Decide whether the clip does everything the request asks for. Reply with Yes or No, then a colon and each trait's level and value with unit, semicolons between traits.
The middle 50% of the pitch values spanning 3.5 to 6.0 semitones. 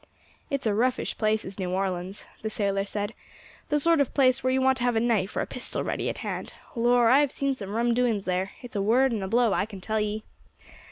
Yes: average, 4.1 semitones